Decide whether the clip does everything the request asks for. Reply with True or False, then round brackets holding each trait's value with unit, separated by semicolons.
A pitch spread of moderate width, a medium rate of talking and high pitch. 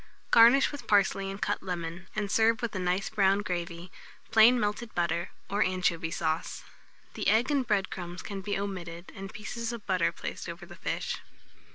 True (3.6 semitones; 180 wpm; 195 Hz)